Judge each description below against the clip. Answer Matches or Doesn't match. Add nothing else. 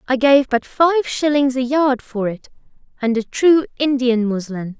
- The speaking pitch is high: Matches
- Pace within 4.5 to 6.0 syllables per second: Doesn't match